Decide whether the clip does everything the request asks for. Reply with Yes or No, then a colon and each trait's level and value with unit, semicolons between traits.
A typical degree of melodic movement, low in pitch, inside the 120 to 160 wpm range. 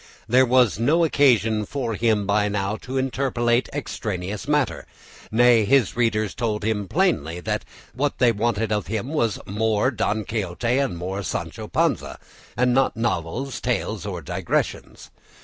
Yes: average, 3.7 semitones; low, 115 Hz; average, 145 wpm